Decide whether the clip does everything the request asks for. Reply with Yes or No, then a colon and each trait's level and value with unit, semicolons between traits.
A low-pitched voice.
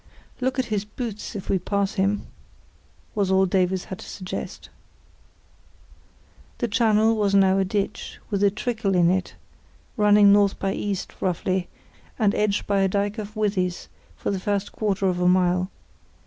No: high, 200 Hz